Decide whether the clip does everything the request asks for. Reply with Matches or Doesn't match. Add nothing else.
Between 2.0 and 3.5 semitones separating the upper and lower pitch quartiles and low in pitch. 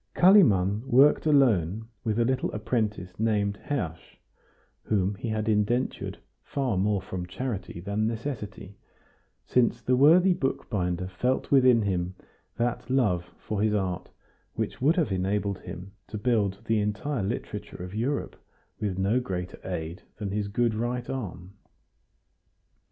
Doesn't match